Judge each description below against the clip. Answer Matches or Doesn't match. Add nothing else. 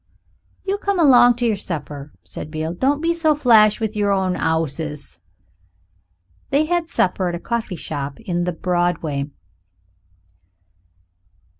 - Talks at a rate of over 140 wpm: Doesn't match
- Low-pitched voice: Doesn't match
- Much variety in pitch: Matches